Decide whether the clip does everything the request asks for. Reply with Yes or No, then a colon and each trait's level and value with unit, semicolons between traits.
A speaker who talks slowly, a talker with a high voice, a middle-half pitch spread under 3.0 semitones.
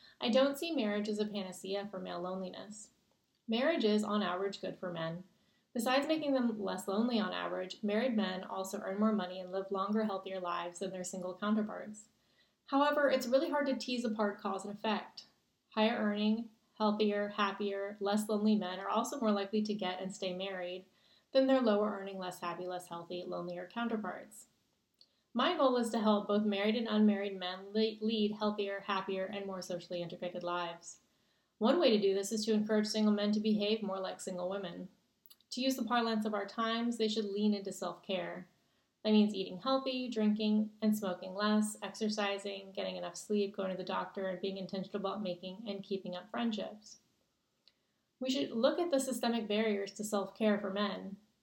No: average, 185 wpm; high, 205 Hz; narrow, 2.5 semitones